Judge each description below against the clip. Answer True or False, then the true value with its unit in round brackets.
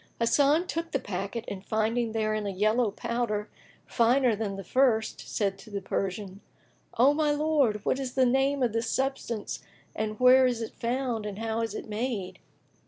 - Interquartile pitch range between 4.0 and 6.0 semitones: False (3.6 semitones)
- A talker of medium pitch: False (230 Hz)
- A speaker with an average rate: True (175 wpm)